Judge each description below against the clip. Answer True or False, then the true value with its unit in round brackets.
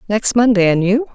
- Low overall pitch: False (215 Hz)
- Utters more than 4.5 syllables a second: True (5.4 syllables/s)